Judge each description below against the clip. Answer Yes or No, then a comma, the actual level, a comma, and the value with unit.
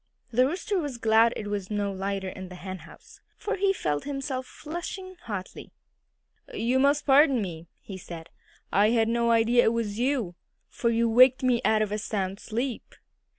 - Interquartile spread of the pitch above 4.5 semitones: Yes, average, 4.9 semitones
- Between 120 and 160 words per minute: No, average, 175 wpm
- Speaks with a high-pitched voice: Yes, high, 230 Hz